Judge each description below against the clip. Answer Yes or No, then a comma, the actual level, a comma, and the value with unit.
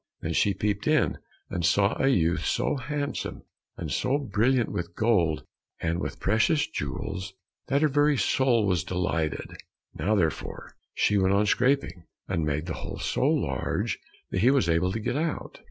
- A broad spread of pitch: Yes, wide, 7.2 semitones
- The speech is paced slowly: No, average, 170 wpm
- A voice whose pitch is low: Yes, low, 100 Hz